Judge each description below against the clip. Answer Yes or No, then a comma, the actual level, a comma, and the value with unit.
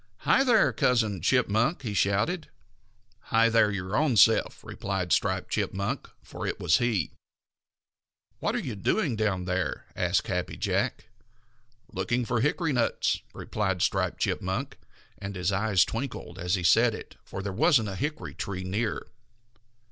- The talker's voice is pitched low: Yes, low, 105 Hz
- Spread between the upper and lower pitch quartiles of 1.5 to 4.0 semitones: No, average, 4.4 semitones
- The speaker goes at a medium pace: Yes, average, 150 wpm